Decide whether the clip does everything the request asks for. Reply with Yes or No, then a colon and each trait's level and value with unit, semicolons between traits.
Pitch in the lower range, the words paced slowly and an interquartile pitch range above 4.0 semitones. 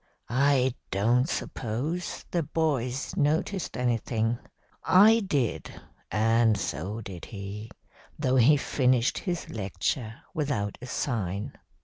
Yes: low, 125 Hz; slow, 105 wpm; average, 4.9 semitones